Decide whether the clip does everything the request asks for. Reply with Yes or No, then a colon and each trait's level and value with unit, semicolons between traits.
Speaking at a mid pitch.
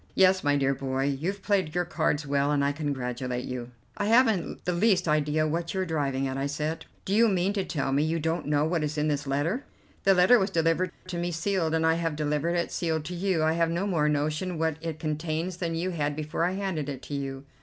Yes: medium, 160 Hz